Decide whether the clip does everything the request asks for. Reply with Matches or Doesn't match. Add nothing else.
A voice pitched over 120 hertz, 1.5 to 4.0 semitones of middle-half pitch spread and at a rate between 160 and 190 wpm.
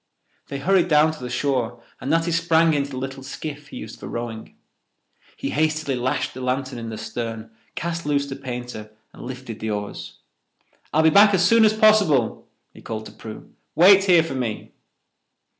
Doesn't match